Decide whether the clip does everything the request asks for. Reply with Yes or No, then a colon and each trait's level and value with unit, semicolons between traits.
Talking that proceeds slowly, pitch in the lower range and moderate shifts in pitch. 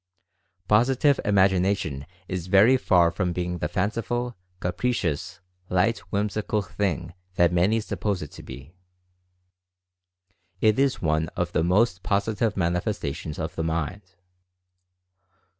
Yes: slow, 115 wpm; very low, 95 Hz; average, 3.9 semitones